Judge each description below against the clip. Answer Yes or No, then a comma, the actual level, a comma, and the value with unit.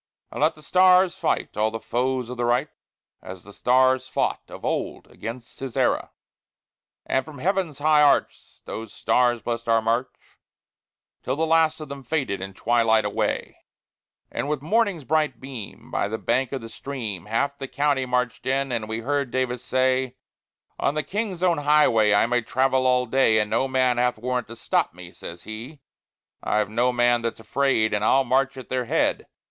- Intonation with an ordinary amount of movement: Yes, average, 3.5 semitones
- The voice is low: Yes, low, 130 Hz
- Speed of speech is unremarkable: Yes, average, 185 wpm